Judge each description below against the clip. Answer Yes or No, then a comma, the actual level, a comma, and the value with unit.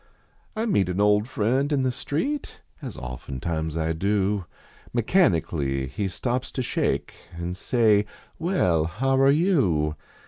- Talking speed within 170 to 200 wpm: No, average, 140 wpm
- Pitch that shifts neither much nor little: No, wide, 8.4 semitones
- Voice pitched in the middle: No, low, 105 Hz